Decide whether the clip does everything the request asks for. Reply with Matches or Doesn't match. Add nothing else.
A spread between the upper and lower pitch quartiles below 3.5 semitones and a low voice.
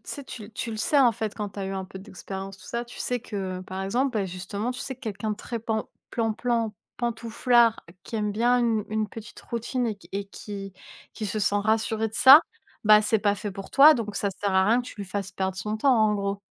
Doesn't match